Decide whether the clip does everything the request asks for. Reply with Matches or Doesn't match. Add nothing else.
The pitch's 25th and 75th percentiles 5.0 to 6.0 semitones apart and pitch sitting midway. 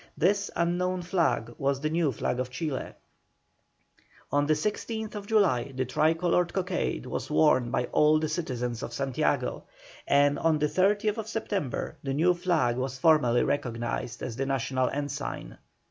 Matches